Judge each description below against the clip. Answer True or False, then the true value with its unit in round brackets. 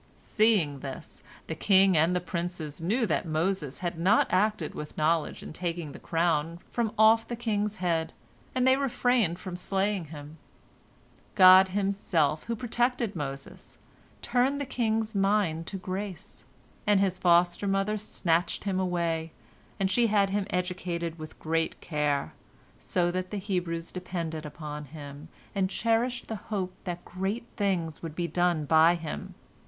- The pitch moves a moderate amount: True (4.0 semitones)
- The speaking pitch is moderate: True (180 Hz)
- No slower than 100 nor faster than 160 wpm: True (150 wpm)